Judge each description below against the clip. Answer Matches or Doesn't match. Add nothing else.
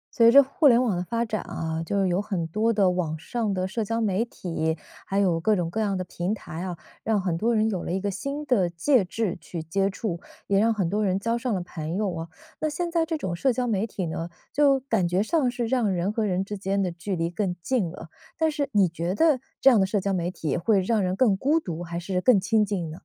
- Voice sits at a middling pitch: Doesn't match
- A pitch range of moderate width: Matches